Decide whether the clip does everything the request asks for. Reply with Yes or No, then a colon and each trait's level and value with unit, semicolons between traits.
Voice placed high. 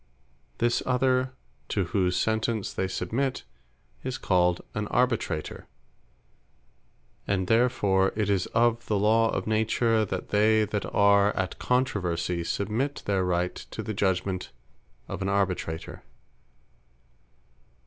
No: low, 105 Hz